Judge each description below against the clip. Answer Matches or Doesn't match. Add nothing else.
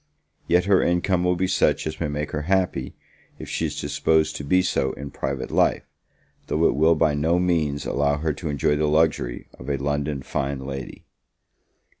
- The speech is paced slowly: Doesn't match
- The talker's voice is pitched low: Matches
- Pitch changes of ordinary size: Matches